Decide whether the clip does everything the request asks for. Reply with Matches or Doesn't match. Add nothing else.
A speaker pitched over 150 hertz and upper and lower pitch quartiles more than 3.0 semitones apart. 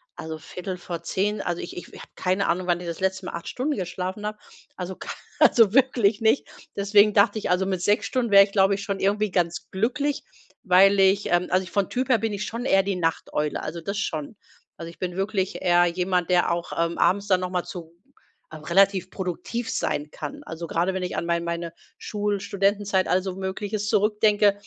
Doesn't match